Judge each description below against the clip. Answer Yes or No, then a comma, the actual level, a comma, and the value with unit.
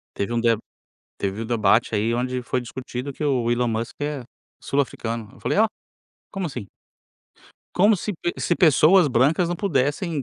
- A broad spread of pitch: Yes, wide, 5.8 semitones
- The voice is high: No, low, 130 Hz